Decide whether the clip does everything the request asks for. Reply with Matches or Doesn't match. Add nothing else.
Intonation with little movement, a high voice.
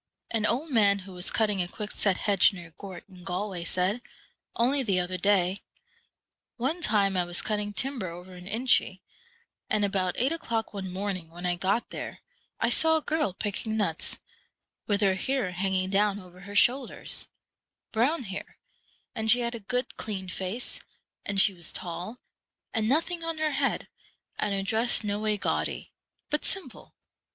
Doesn't match